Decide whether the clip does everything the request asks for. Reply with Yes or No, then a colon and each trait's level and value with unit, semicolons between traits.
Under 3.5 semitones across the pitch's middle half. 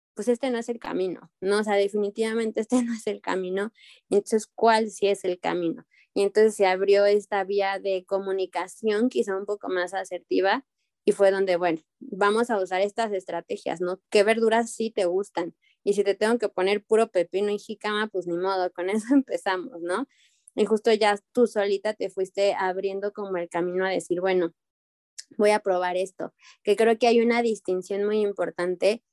Yes: average, 2.8 semitones